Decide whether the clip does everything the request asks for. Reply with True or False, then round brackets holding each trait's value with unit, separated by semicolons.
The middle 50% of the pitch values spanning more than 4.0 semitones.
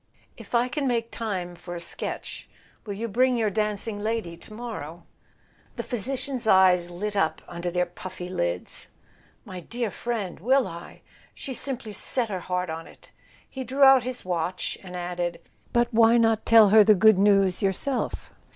True (4.8 semitones)